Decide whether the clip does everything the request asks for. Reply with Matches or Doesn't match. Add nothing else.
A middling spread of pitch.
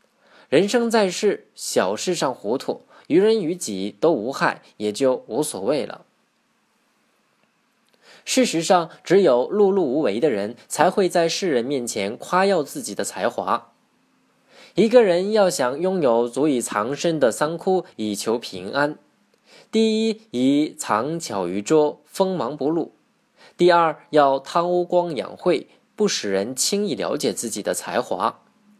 Doesn't match